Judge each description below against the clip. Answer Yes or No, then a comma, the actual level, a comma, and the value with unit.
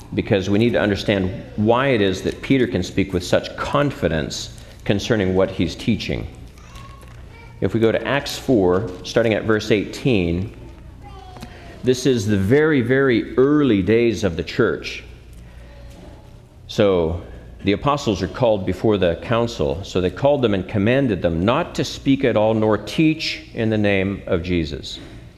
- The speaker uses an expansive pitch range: No, average, 4.6 semitones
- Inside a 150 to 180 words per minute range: Yes, average, 155 wpm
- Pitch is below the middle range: Yes, low, 105 Hz